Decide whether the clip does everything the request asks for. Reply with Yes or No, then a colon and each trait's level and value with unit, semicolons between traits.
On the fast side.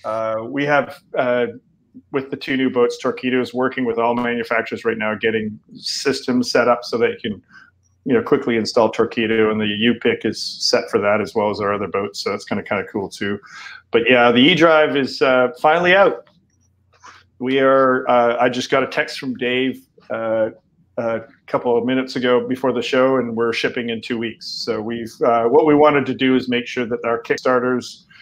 Yes: fast, 215 wpm